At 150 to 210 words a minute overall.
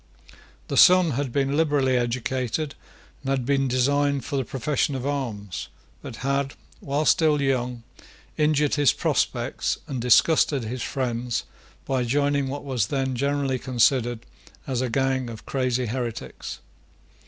No: average, 140 wpm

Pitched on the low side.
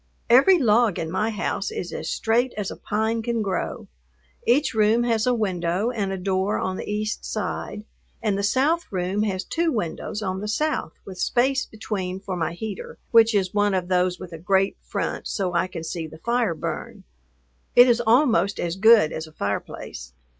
No: high, 205 Hz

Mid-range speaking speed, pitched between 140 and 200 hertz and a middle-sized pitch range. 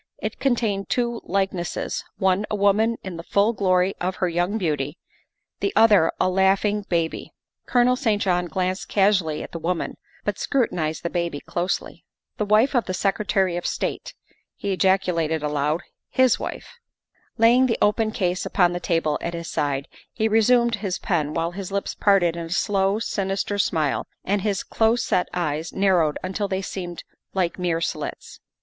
Yes: average, 175 wpm; high, 190 Hz; average, 3.4 semitones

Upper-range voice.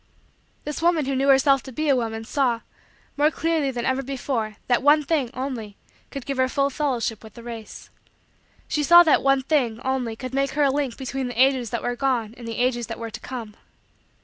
Yes: very high, 260 Hz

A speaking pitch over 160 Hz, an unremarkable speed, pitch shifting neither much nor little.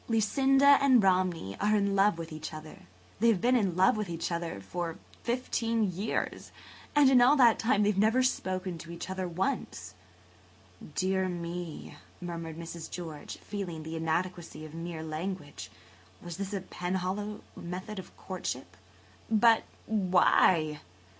Yes: medium, 185 Hz; average, 150 wpm; average, 4.1 semitones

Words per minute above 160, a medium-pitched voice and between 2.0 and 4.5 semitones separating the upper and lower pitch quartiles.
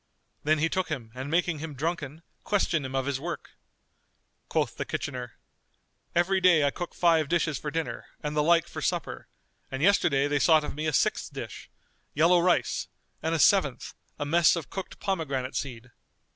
Yes: average, 180 wpm; medium, 155 Hz; average, 3.5 semitones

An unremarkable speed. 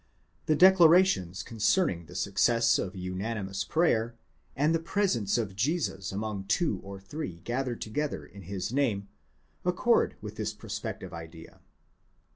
No: slow, 130 wpm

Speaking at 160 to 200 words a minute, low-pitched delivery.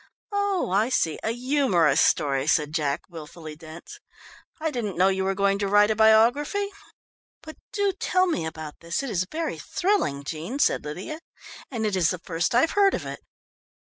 No: average, 180 wpm; high, 200 Hz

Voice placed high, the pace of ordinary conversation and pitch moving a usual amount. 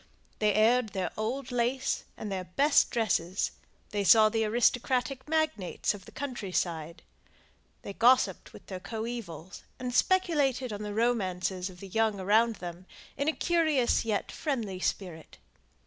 Yes: high, 220 Hz; average, 145 wpm; average, 4.9 semitones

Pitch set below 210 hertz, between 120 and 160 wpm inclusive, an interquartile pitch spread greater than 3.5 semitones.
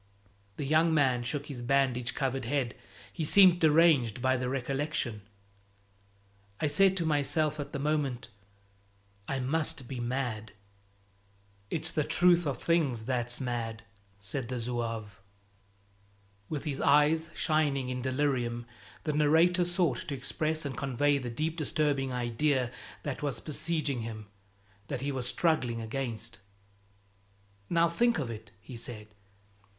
Yes: low, 135 Hz; slow, 135 wpm; average, 4.2 semitones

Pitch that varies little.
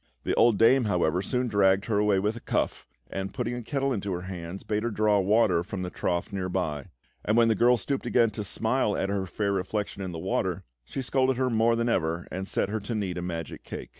No: average, 3.9 semitones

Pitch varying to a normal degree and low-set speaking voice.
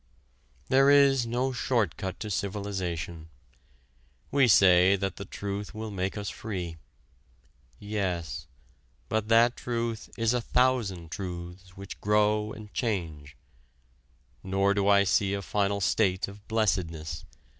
Yes: average, 3.1 semitones; low, 100 Hz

